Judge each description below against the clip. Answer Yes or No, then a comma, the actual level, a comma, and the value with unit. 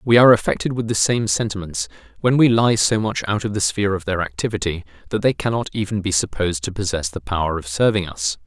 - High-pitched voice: No, low, 100 Hz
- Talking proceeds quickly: Yes, fast, 225 wpm